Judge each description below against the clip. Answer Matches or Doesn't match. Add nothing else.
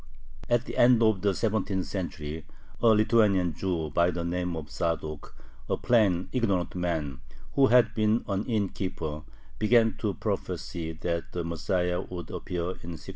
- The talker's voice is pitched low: Matches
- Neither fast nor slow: Matches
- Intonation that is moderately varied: Matches